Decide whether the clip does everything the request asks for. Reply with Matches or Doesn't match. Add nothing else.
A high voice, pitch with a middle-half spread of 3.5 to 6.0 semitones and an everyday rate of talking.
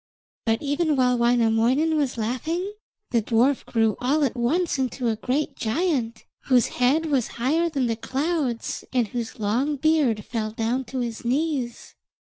Matches